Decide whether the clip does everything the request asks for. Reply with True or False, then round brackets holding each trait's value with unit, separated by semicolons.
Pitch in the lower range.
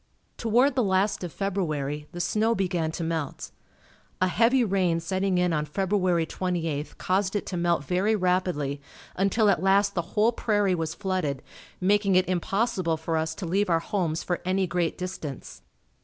False (185 Hz)